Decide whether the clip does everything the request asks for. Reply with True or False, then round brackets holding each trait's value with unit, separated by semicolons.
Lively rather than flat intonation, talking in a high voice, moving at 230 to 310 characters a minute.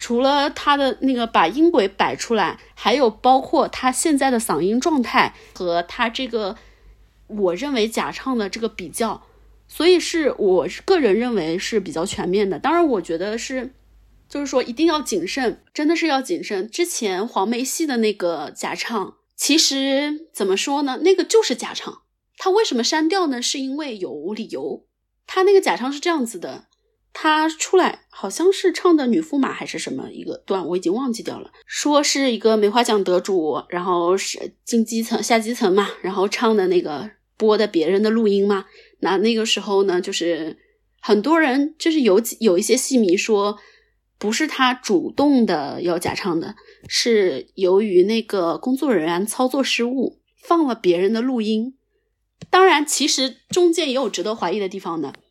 True (7.1 semitones; 250 Hz; 260 characters per minute)